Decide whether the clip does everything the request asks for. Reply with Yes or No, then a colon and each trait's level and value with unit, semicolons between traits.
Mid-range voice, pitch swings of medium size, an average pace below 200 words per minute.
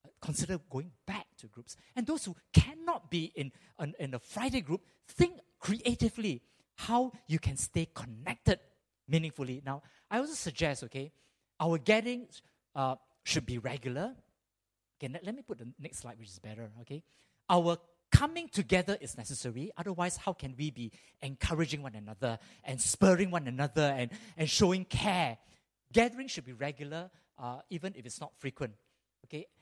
No: medium, 150 Hz; wide, 6.0 semitones; average, 155 wpm